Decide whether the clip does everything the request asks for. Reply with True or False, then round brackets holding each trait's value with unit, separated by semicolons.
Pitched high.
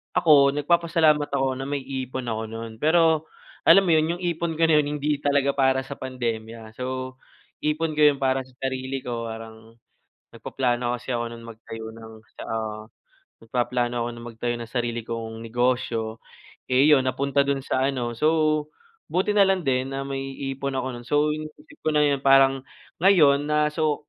False (135 Hz)